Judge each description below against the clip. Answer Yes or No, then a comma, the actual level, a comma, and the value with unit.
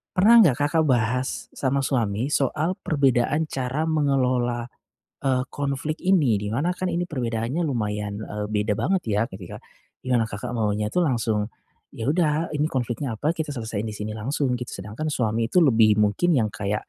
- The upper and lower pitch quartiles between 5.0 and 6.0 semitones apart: Yes, wide, 5.6 semitones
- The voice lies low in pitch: Yes, low, 125 Hz